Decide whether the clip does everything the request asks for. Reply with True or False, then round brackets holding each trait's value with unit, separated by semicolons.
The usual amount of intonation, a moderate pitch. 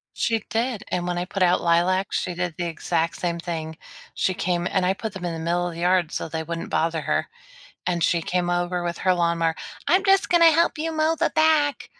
True (4.1 semitones; 175 Hz)